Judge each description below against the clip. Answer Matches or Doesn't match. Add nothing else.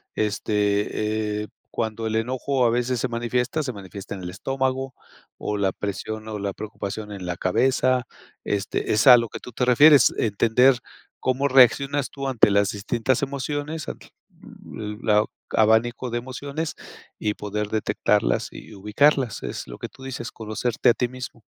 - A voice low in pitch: Matches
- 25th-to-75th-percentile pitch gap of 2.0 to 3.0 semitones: Doesn't match